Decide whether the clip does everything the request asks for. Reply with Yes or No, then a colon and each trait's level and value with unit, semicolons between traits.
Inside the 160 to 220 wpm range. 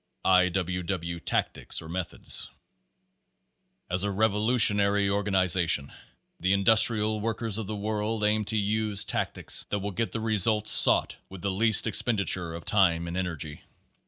No: average, 145 wpm